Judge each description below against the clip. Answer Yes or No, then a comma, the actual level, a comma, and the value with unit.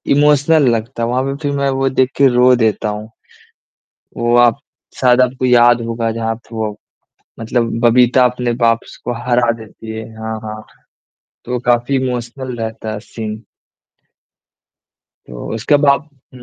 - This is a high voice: No, low, 120 Hz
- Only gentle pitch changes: Yes, narrow, 2.3 semitones